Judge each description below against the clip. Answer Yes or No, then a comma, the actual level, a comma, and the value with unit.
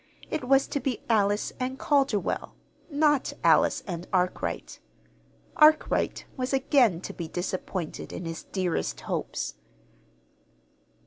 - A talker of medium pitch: No, high, 240 Hz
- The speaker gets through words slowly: Yes, slow, 115 wpm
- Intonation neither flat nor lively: No, wide, 7.0 semitones